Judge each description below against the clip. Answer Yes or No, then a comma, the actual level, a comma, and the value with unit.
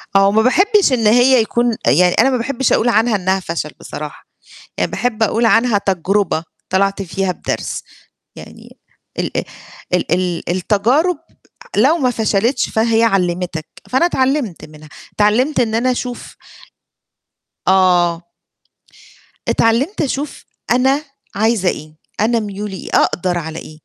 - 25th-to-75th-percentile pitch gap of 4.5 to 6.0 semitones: Yes, average, 5.1 semitones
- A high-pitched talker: Yes, high, 220 Hz